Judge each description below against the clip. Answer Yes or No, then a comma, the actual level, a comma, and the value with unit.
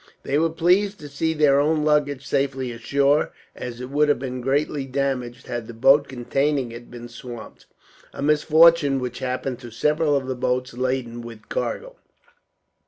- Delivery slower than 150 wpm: No, average, 170 wpm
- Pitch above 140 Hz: No, low, 135 Hz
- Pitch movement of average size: Yes, average, 3.1 semitones